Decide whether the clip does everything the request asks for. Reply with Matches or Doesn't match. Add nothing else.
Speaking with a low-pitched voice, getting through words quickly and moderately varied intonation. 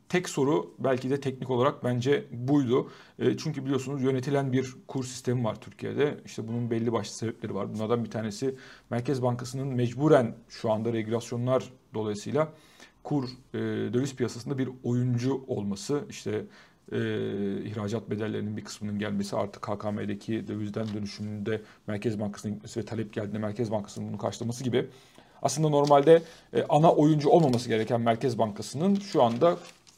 Matches